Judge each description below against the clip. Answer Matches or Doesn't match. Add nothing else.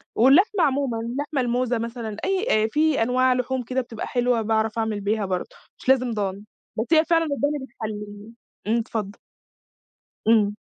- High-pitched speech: Matches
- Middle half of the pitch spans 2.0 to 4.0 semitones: Matches